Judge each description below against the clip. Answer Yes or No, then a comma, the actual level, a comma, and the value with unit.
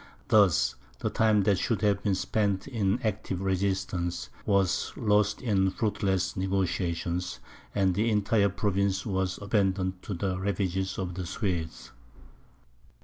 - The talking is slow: Yes, slow, 130 wpm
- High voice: No, very low, 95 Hz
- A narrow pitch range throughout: Yes, narrow, 1.8 semitones